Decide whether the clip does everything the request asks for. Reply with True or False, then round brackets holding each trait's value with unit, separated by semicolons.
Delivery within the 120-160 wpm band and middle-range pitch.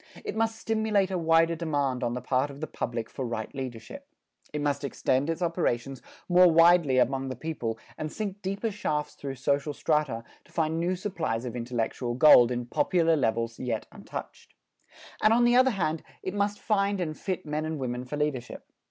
False (185 wpm; 150 Hz)